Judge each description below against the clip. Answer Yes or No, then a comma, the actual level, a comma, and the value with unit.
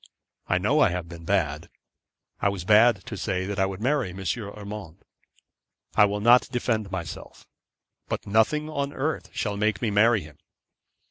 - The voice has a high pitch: No, low, 105 Hz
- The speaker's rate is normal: Yes, average, 170 wpm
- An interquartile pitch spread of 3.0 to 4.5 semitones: Yes, average, 3.9 semitones